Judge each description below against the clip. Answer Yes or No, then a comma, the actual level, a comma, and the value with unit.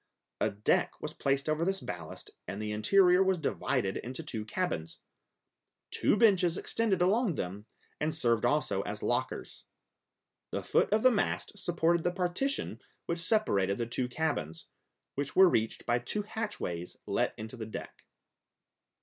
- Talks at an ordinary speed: Yes, average, 150 wpm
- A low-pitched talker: No, medium, 160 Hz